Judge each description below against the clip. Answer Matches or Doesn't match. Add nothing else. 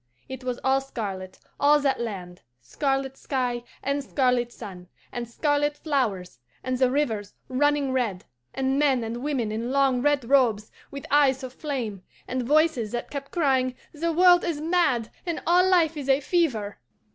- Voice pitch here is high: Matches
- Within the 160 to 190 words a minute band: Matches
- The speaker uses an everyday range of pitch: Matches